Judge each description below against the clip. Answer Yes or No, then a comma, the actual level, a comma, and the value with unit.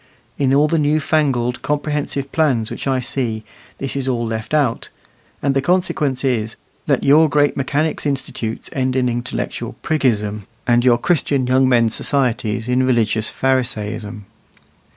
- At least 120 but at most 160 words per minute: Yes, average, 150 wpm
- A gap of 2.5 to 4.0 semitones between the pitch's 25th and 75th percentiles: Yes, average, 3.5 semitones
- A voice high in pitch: No, low, 130 Hz